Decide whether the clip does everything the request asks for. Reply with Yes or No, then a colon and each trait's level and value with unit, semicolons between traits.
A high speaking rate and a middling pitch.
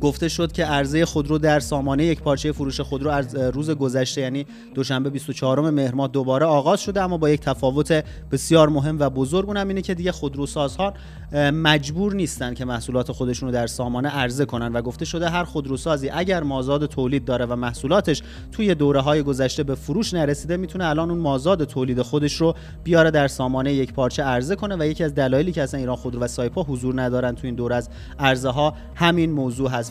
Yes: fast, 195 wpm; medium, 145 Hz